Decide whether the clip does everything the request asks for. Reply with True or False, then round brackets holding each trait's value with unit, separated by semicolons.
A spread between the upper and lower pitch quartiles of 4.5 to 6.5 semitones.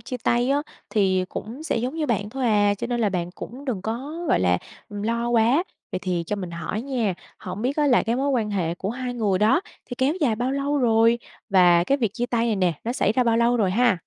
False (4.1 semitones)